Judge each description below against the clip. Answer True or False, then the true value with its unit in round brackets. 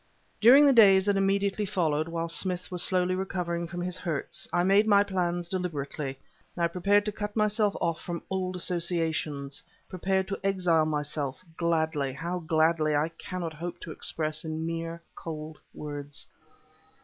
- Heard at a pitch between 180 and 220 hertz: False (170 Hz)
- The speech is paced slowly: False (155 wpm)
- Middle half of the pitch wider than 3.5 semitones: False (3.2 semitones)